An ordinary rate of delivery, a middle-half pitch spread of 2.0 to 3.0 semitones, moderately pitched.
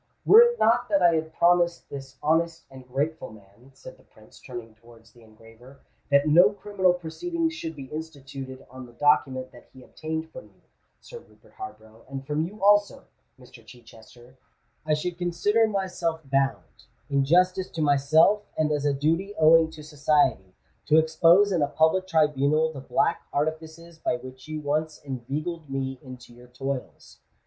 No: average, 170 wpm; average, 4.2 semitones; medium, 150 Hz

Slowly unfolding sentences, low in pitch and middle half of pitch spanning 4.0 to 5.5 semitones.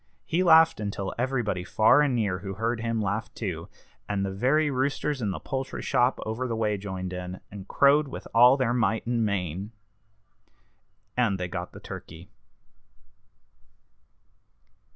No: average, 150 wpm; low, 110 Hz; average, 4.9 semitones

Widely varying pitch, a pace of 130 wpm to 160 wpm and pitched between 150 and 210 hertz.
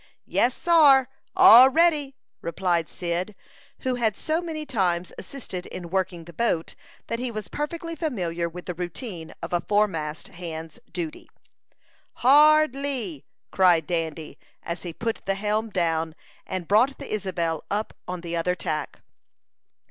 Yes: wide, 7.0 semitones; average, 145 wpm; high, 190 Hz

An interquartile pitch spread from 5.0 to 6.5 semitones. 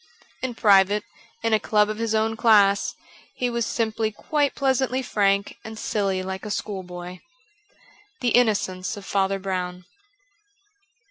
No: average, 2.9 semitones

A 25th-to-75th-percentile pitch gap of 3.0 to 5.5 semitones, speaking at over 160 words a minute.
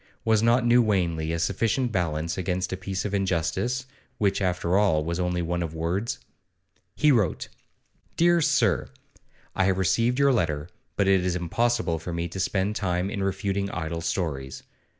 Yes: average, 4.2 semitones; average, 170 wpm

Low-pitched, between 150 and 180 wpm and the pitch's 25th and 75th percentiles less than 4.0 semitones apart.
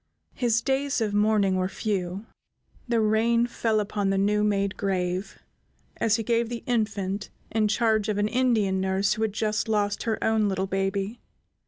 No: high, 210 Hz; average, 170 wpm; narrow, 2.4 semitones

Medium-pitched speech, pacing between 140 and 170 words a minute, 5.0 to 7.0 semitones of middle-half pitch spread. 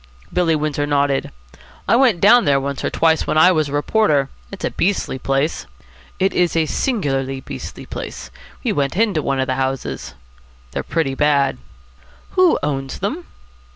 Yes: medium, 150 Hz; average, 165 wpm; average, 5.3 semitones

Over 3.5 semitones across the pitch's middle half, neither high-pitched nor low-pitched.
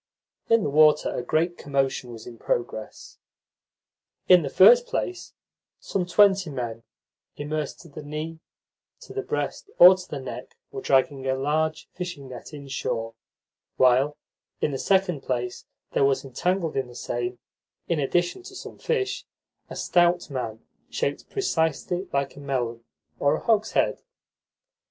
Yes: average, 5.2 semitones; medium, 150 Hz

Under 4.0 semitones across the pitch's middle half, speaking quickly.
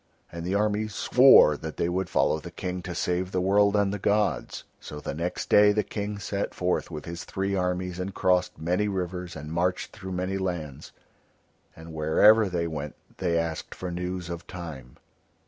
No: average, 2.7 semitones; average, 185 wpm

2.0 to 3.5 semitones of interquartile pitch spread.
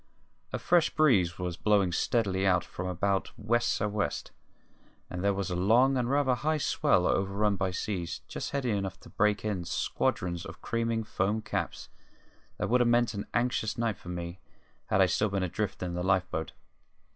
No: average, 4.1 semitones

